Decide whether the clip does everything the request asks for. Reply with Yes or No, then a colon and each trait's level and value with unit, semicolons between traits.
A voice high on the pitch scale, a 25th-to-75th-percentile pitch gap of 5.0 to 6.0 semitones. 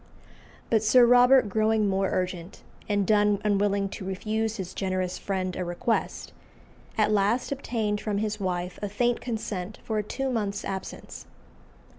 No: high, 205 Hz; narrow, 2.5 semitones